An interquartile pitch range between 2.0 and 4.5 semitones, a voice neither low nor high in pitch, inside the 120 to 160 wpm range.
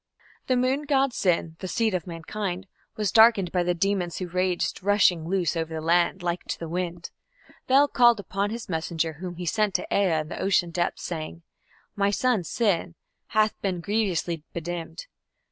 No: average, 3.7 semitones; medium, 180 Hz; average, 180 wpm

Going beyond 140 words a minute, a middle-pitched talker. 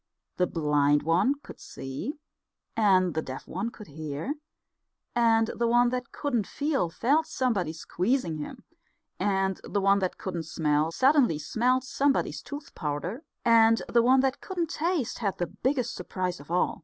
No: average, 155 wpm; high, 215 Hz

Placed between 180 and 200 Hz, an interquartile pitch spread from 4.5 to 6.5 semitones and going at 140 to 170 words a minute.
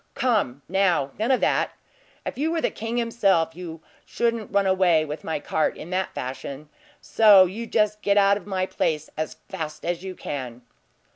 No: medium, 185 Hz; average, 5.2 semitones; average, 185 wpm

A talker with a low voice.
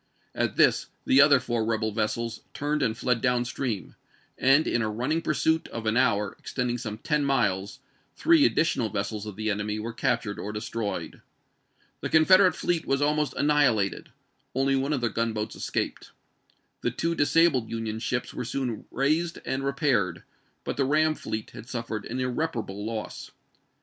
Yes: low, 125 Hz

